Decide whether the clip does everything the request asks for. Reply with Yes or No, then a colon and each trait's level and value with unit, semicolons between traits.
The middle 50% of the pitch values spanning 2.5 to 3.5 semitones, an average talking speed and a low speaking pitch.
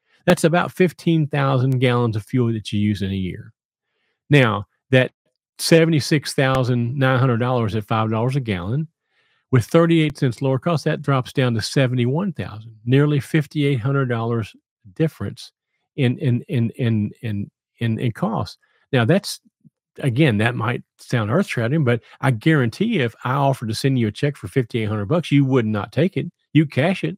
No: average, 4.3 semitones; average, 155 wpm; low, 130 Hz